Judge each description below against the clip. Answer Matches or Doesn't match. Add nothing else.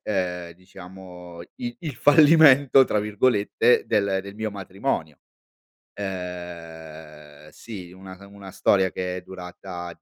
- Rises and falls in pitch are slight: Doesn't match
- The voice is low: Matches